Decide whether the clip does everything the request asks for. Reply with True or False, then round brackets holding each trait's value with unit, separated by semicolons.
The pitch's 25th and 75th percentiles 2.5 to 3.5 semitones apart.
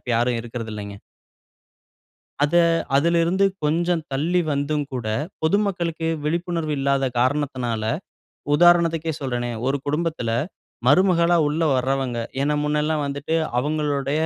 False (3.9 semitones)